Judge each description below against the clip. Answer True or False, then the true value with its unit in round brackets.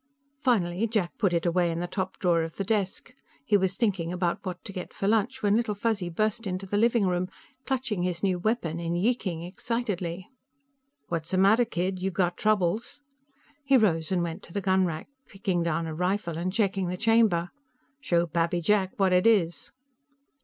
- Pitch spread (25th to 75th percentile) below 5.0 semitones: True (3.6 semitones)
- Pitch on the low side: False (185 Hz)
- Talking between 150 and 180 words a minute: False (190 wpm)